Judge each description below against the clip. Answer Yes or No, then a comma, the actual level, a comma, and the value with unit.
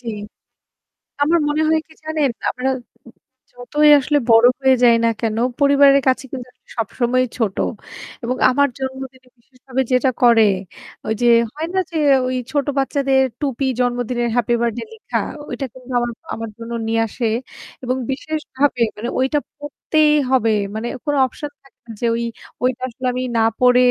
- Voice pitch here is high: Yes, very high, 255 Hz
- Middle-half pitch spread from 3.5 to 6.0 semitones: No, average, 2.8 semitones